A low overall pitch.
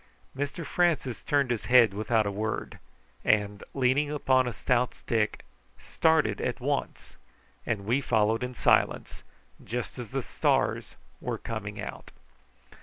Yes: low, 120 Hz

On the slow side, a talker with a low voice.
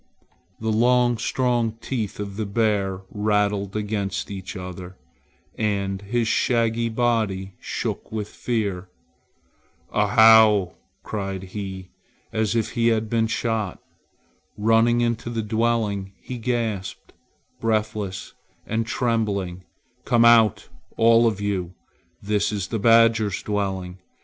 Yes: slow, 115 wpm; low, 110 Hz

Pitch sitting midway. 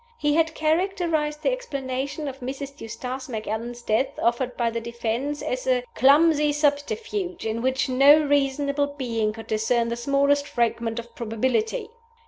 No: very high, 270 Hz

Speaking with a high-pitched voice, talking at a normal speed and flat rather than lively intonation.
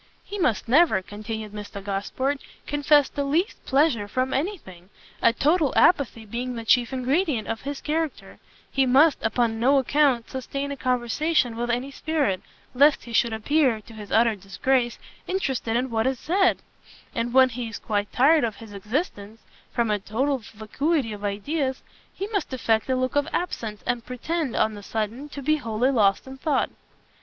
No: very high, 250 Hz; average, 175 wpm; average, 4.5 semitones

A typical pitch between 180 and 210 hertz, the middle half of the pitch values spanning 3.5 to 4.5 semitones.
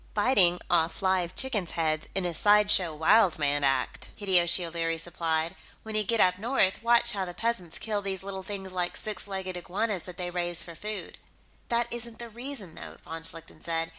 Yes: medium, 185 Hz; average, 3.8 semitones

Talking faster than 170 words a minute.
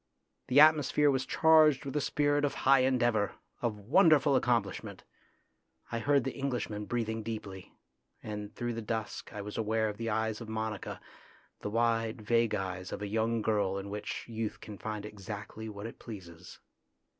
No: average, 165 wpm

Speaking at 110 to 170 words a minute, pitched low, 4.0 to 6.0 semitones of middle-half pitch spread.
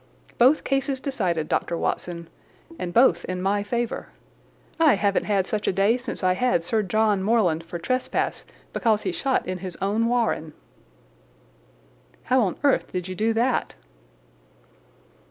No: average, 150 wpm; high, 210 Hz; average, 4.9 semitones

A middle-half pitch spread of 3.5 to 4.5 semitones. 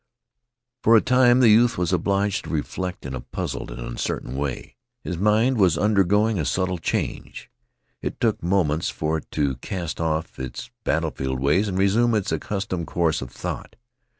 No: average, 5.2 semitones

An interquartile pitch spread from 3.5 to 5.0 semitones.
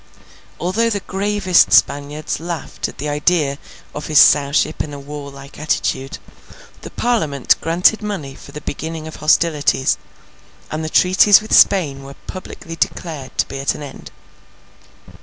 Yes: average, 4.1 semitones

